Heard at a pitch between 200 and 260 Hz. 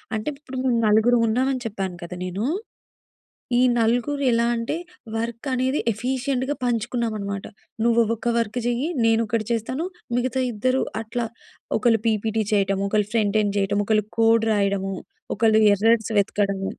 Yes: high, 225 Hz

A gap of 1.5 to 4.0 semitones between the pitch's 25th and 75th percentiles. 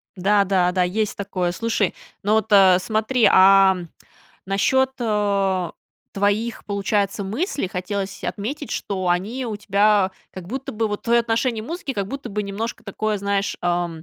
Yes: average, 2.7 semitones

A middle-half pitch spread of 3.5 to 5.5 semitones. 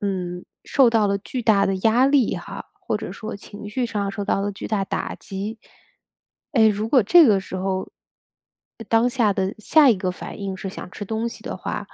No: average, 2.8 semitones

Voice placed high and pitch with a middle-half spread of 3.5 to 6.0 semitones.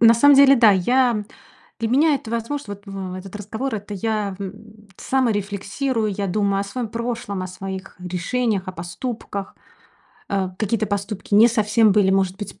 No: high, 210 Hz; average, 3.0 semitones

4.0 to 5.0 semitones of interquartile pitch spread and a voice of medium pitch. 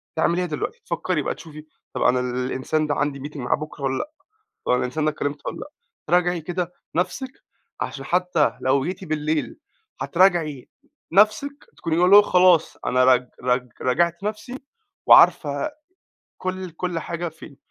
Yes: average, 4.3 semitones; medium, 165 Hz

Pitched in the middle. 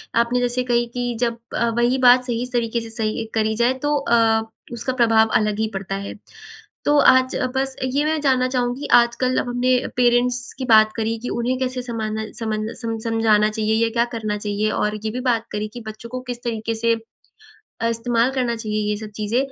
No: high, 235 Hz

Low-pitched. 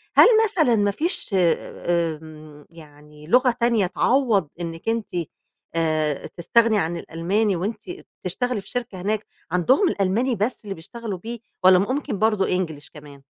No: high, 195 Hz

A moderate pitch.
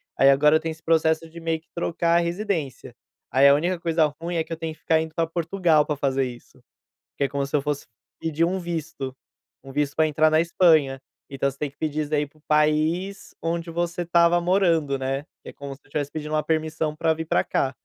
Yes: medium, 155 Hz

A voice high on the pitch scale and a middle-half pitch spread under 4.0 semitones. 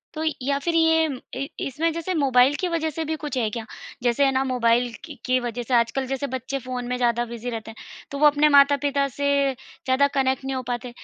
Yes: very high, 265 Hz; average, 2.8 semitones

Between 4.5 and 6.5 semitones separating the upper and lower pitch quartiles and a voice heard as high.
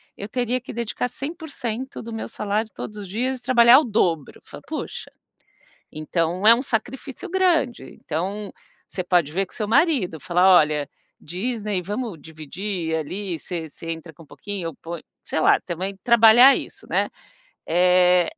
Yes: wide, 5.6 semitones; high, 200 Hz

